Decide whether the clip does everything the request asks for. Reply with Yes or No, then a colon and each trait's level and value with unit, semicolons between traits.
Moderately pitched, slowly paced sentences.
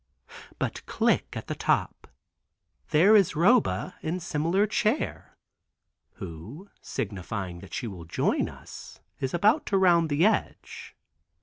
Yes: medium, 165 Hz; slow, 125 wpm